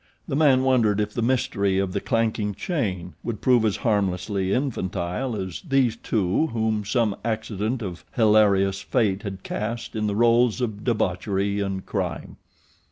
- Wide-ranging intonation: No, average, 3.2 semitones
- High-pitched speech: No, low, 105 Hz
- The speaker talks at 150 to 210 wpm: Yes, average, 155 wpm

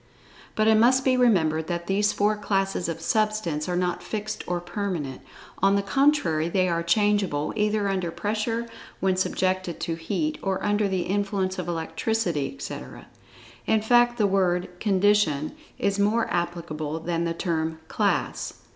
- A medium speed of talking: Yes, average, 155 wpm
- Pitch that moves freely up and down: No, average, 3.7 semitones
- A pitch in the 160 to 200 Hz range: Yes, high, 190 Hz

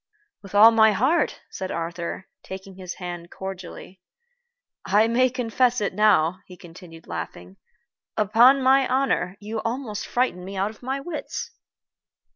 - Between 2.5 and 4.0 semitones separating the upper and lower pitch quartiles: No, average, 5.3 semitones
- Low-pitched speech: No, high, 205 Hz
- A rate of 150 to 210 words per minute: No, average, 140 wpm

